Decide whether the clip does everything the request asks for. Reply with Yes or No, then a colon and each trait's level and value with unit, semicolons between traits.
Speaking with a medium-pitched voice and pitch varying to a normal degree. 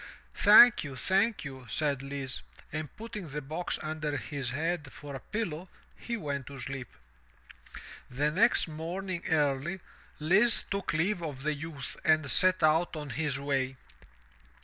Yes: medium, 155 Hz; average, 4.1 semitones